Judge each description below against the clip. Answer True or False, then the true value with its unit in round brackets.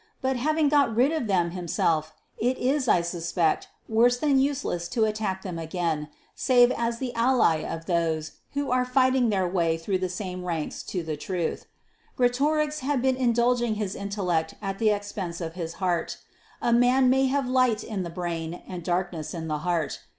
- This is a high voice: True (205 Hz)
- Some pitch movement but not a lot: False (6.7 semitones)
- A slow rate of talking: False (185 wpm)